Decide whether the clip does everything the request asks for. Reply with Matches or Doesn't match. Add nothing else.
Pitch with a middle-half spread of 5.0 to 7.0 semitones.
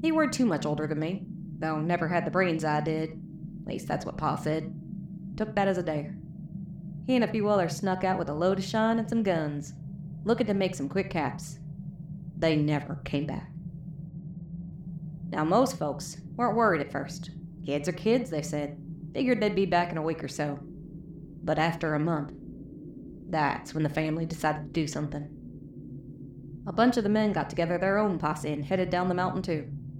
Doesn't match